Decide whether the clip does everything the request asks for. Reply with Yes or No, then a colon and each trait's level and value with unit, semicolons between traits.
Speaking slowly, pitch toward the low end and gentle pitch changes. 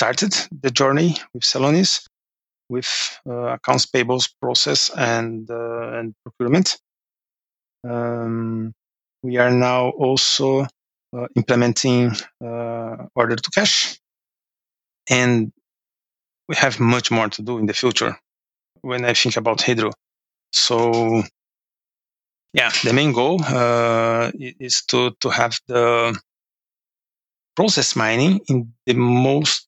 Yes: slow, 115 wpm; low, 120 Hz; narrow, 1.8 semitones